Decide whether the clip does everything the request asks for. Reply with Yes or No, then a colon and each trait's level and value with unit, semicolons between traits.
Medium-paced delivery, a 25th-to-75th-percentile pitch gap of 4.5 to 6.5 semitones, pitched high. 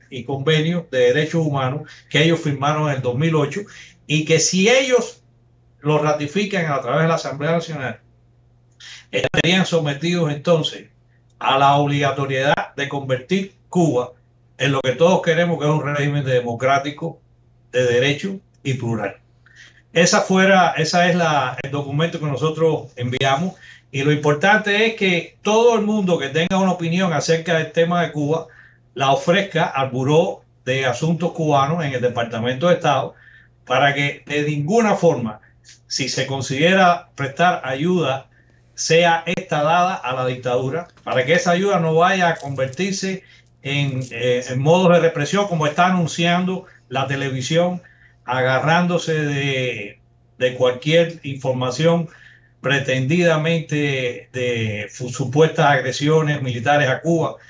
No: average, 140 wpm; average, 4.8 semitones; medium, 145 Hz